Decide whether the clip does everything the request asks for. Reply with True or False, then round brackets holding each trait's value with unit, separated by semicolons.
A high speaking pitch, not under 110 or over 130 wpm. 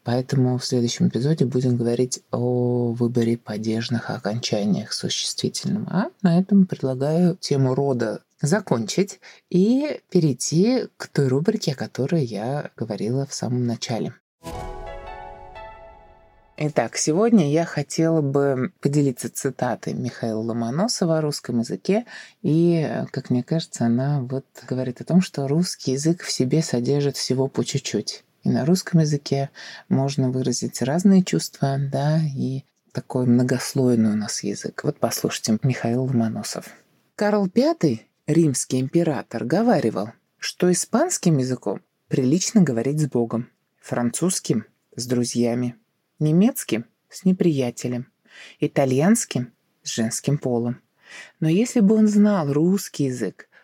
False (140 Hz; 120 wpm)